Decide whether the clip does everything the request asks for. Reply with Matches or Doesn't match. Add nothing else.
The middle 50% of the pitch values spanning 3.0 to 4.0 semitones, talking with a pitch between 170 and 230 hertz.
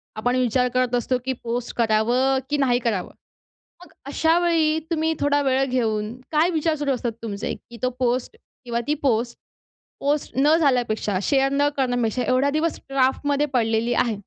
Doesn't match